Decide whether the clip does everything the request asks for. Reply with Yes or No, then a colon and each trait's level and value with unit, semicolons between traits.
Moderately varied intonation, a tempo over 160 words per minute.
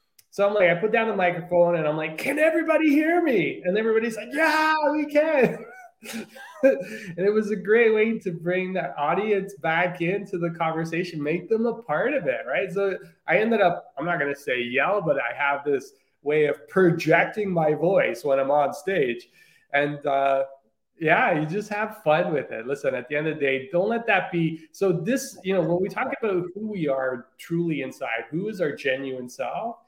No: wide, 6.2 semitones; fast, 205 wpm